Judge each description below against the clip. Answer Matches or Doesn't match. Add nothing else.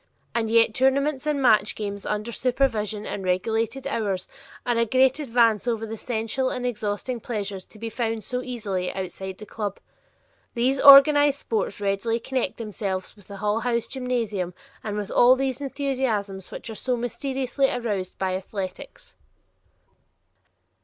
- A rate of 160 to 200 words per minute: Doesn't match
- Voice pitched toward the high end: Matches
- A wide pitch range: Doesn't match